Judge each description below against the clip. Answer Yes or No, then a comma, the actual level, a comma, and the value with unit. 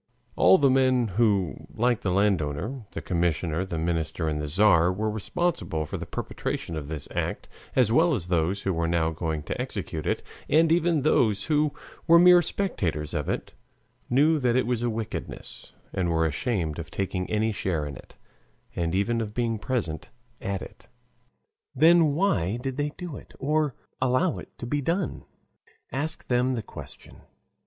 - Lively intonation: Yes, wide, 8.1 semitones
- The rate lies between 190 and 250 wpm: No, average, 175 wpm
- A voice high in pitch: No, low, 110 Hz